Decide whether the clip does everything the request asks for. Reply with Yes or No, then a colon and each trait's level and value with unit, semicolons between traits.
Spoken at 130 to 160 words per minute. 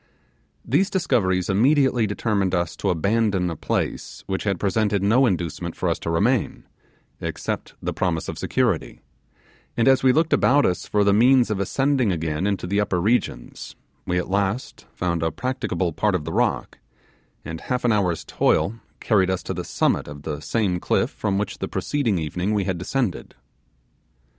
No: average, 175 wpm